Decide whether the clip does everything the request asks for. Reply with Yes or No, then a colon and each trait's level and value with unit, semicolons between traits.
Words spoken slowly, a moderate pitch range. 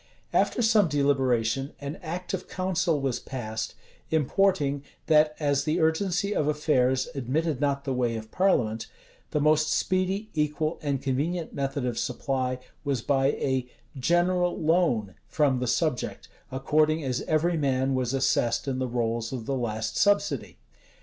No: average, 150 wpm; average, 4.0 semitones